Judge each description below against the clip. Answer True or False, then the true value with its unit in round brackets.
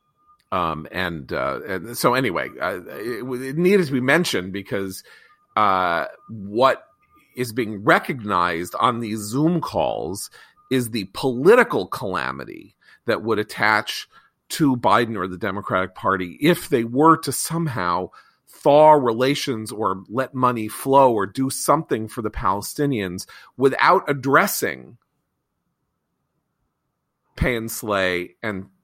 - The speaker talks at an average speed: False (125 wpm)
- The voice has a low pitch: True (120 Hz)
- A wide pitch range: True (6.9 semitones)